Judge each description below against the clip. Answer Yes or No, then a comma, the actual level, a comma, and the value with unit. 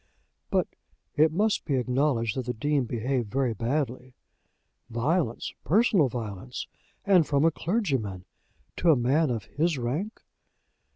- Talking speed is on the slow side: Yes, slow, 130 wpm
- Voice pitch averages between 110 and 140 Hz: Yes, low, 135 Hz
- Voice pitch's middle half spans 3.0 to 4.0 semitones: No, average, 5.0 semitones